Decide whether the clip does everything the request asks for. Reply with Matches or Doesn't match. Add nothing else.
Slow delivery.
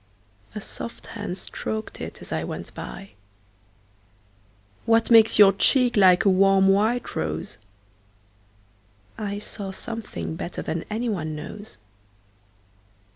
Matches